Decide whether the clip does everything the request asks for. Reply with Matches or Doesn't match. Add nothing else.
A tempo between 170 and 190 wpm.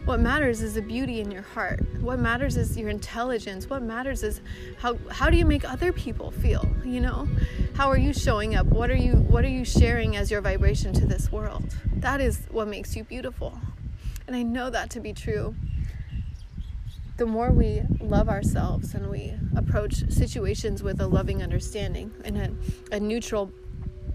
Matches